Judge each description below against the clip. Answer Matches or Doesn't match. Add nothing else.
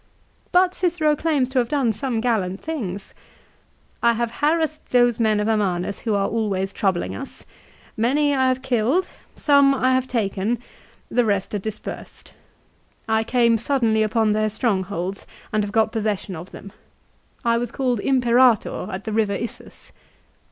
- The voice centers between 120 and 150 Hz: Doesn't match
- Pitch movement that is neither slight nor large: Matches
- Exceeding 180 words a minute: Doesn't match